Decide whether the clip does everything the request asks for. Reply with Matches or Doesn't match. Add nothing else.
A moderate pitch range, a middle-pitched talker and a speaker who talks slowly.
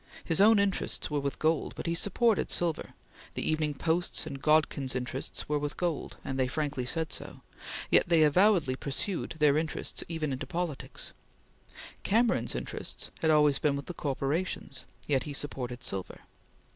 Doesn't match